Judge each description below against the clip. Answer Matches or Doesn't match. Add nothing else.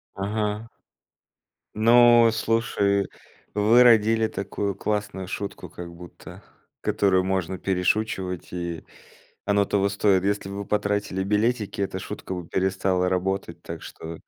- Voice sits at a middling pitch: Doesn't match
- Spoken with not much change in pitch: Matches